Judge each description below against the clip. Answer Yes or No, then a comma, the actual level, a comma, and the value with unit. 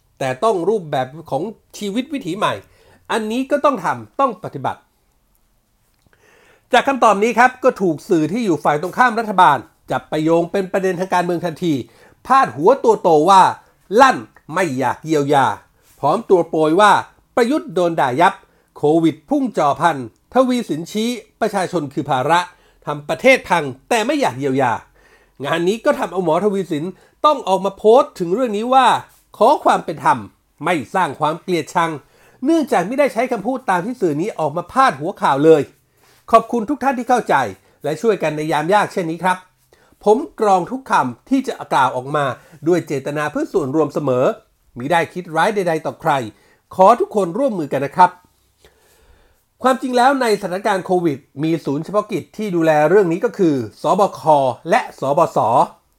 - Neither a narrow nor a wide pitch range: No, wide, 7.4 semitones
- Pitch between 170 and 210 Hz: Yes, high, 190 Hz